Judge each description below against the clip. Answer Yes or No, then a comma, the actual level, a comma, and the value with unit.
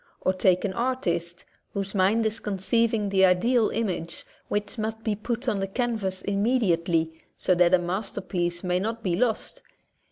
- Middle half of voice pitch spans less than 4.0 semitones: Yes, average, 3.6 semitones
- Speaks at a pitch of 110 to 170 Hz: No, high, 195 Hz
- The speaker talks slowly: No, average, 160 wpm